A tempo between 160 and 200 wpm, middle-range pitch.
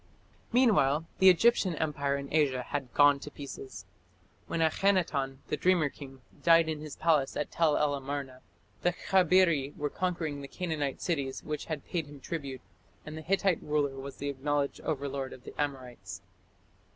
Yes: average, 165 wpm; medium, 145 Hz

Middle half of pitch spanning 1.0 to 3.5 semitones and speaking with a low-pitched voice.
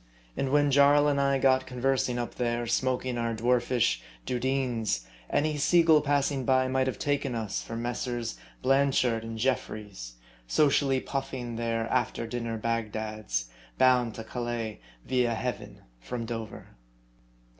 Yes: average, 2.9 semitones; low, 125 Hz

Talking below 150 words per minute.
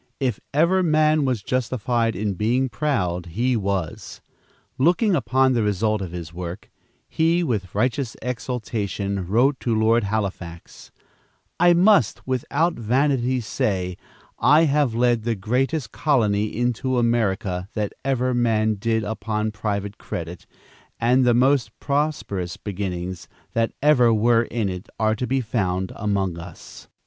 Yes: slow, 135 wpm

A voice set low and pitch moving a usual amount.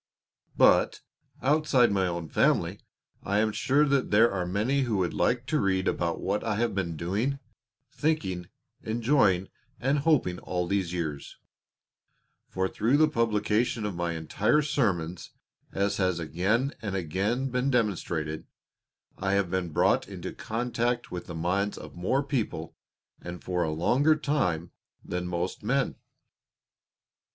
No: low, 100 Hz; wide, 5.8 semitones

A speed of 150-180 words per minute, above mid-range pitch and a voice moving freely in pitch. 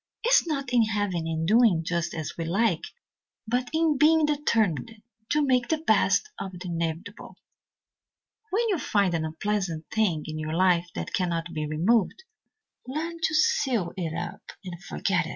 Yes: average, 170 wpm; high, 195 Hz; wide, 8.0 semitones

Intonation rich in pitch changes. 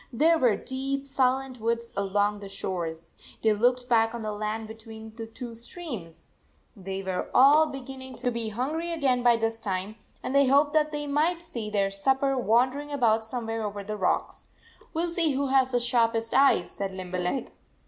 No: average, 4.3 semitones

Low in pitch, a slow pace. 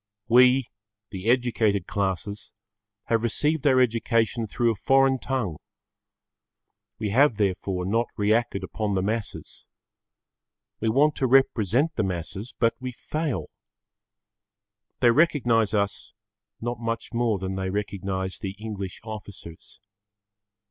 Yes: low, 110 Hz; slow, 120 wpm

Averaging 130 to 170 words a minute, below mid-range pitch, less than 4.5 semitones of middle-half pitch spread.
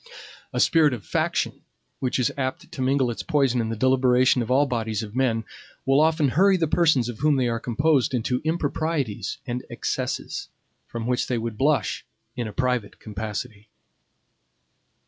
Yes: average, 165 wpm; low, 125 Hz; average, 3.6 semitones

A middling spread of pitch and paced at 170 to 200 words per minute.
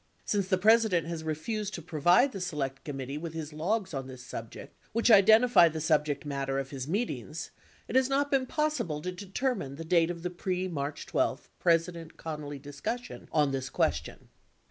No: wide, 5.8 semitones; average, 185 wpm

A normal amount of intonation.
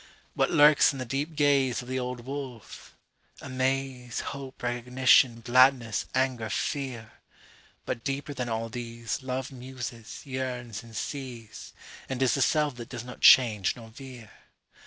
No: narrow, 2.3 semitones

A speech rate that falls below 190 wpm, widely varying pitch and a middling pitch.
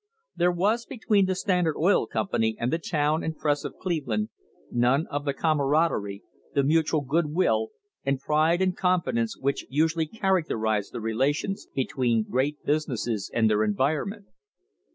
Yes: average, 155 wpm; wide, 6.0 semitones; medium, 150 Hz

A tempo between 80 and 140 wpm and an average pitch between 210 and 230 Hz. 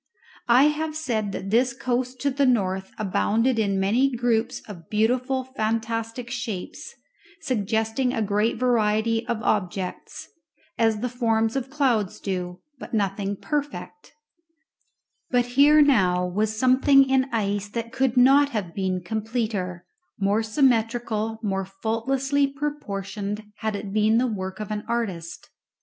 Yes: slow, 135 wpm; high, 225 Hz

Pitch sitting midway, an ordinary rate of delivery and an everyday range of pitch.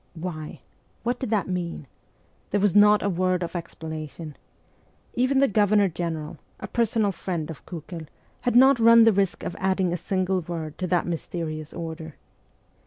Yes: medium, 180 Hz; average, 165 wpm; average, 4.0 semitones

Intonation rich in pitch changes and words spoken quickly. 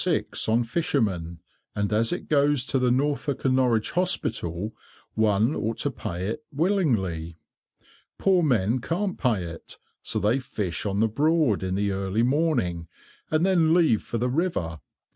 No: wide, 7.0 semitones; average, 155 wpm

